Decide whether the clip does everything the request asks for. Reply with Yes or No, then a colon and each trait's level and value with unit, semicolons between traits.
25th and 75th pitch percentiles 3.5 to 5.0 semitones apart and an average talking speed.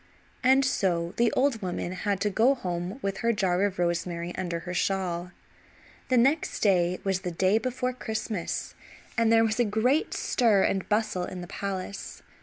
Yes: average, 4.2 semitones; average, 175 wpm